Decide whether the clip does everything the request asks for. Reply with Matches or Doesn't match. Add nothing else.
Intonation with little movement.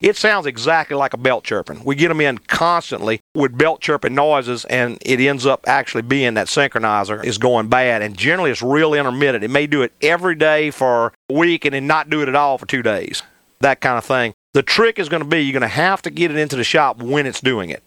Doesn't match